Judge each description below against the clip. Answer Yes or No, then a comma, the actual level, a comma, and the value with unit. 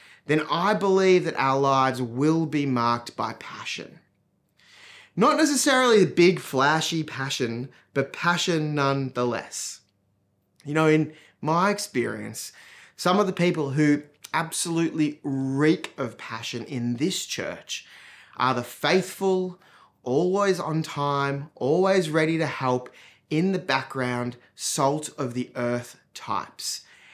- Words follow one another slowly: Yes, slow, 120 wpm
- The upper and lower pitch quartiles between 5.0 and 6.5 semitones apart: Yes, wide, 5.4 semitones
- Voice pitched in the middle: Yes, medium, 150 Hz